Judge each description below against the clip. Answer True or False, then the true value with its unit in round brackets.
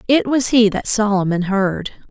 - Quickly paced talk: False (170 wpm)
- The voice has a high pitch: True (215 Hz)